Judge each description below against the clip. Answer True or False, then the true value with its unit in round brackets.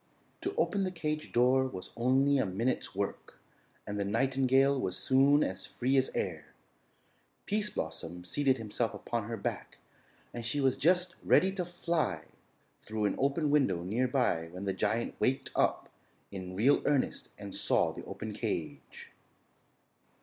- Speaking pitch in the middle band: False (130 Hz)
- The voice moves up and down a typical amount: False (5.9 semitones)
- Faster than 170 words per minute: False (155 wpm)